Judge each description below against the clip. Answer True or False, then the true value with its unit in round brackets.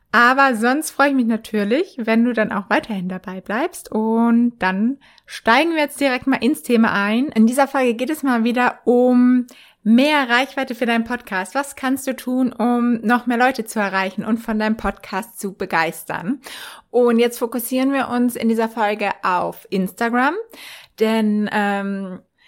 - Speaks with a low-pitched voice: False (240 Hz)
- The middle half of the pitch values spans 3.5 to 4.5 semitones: False (3.1 semitones)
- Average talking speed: True (170 wpm)